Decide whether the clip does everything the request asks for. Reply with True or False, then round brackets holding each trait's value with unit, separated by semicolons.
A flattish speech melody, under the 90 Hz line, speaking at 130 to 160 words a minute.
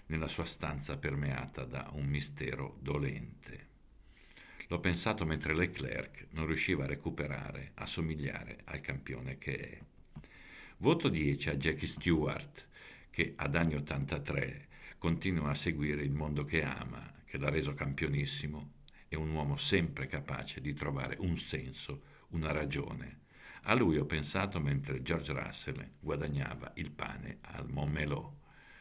True (2.2 semitones; 75 Hz; 135 wpm)